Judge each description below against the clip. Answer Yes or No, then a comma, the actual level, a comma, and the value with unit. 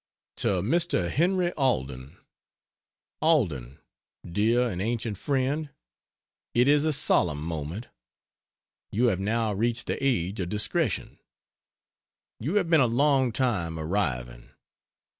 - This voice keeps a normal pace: No, slow, 115 wpm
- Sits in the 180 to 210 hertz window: No, low, 115 Hz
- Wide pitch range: Yes, wide, 8.0 semitones